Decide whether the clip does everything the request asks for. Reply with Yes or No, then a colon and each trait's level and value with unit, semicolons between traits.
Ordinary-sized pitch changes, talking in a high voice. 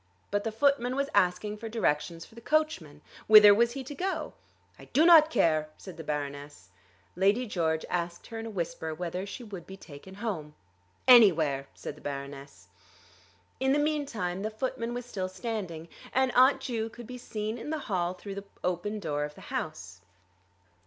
No: wide, 6.6 semitones; high, 205 Hz